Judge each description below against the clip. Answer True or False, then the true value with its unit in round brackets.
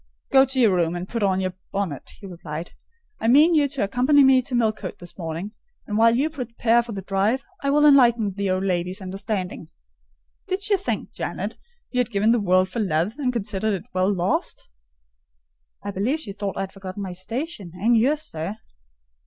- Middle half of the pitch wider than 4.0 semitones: True (5.1 semitones)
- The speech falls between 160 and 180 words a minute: False (195 wpm)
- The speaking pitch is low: False (210 Hz)